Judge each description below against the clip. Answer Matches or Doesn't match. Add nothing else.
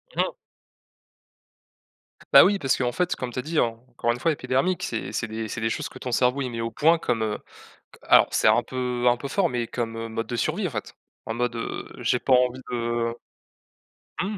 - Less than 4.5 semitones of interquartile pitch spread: Matches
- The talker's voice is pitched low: Matches